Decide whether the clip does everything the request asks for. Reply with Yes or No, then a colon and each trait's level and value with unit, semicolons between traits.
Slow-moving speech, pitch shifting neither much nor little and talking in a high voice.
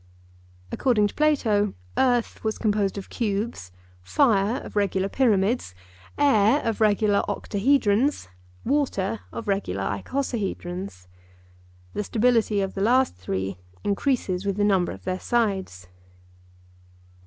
Yes: slow, 115 wpm; average, 3.9 semitones; high, 205 Hz